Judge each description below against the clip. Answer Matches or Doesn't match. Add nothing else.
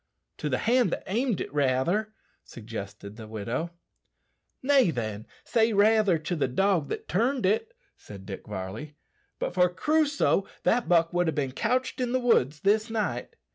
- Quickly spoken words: Doesn't match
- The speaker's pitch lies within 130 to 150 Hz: Doesn't match